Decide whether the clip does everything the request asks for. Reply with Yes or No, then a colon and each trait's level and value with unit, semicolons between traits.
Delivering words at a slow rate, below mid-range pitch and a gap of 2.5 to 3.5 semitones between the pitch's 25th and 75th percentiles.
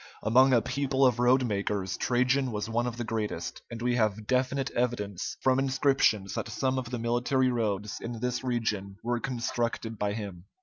No: average, 175 wpm; low, 120 Hz; average, 3.1 semitones